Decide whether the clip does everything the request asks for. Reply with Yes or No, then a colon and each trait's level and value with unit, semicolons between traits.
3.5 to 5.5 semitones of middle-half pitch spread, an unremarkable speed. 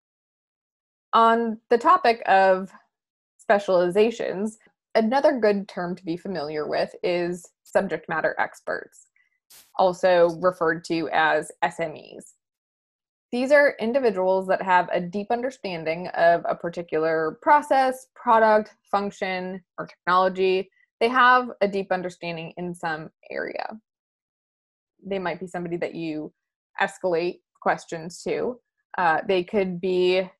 No: average, 4.6 semitones; slow, 115 wpm